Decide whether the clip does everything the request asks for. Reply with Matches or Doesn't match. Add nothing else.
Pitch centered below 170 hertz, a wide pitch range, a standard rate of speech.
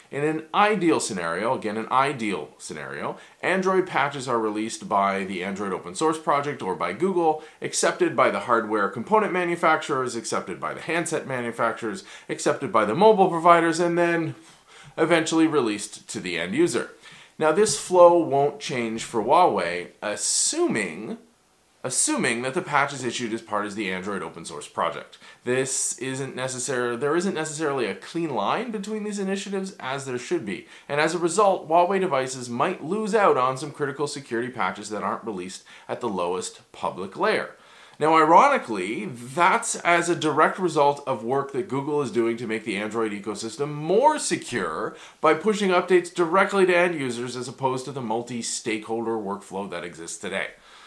Matches